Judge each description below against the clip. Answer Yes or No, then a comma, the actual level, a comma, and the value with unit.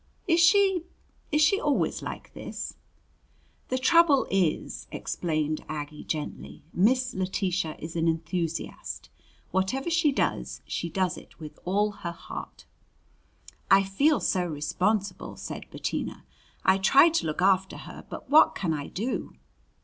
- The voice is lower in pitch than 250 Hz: Yes, high, 190 Hz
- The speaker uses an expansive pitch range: Yes, wide, 8.3 semitones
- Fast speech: No, slow, 135 wpm